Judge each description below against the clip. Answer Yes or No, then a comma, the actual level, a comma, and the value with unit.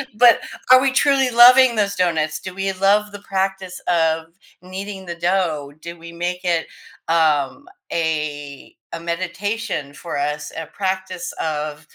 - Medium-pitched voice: Yes, medium, 180 Hz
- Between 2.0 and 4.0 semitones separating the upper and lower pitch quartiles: Yes, average, 3.7 semitones